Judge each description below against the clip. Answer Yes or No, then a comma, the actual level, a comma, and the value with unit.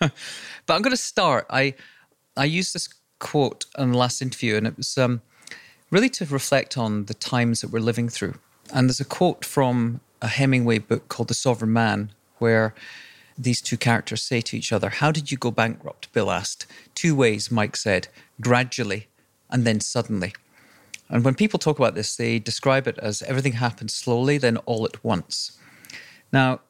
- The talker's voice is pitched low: Yes, low, 120 Hz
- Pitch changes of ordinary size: Yes, average, 3.0 semitones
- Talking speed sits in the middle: Yes, average, 180 wpm